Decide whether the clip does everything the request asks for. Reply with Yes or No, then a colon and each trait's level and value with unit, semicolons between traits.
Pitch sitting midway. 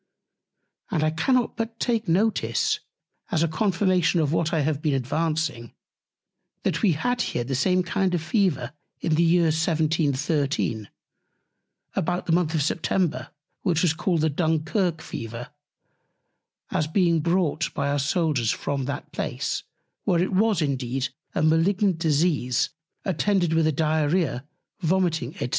Yes: medium, 160 Hz